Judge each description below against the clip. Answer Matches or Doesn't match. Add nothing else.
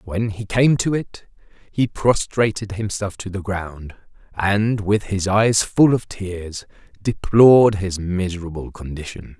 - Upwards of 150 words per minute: Doesn't match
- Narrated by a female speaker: Doesn't match